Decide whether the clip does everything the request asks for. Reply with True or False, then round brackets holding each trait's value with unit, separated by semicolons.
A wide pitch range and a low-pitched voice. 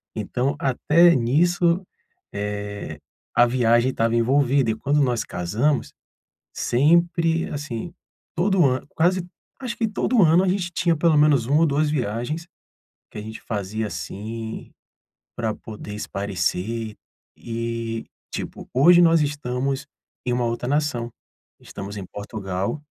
True (6.3 semitones; 125 Hz)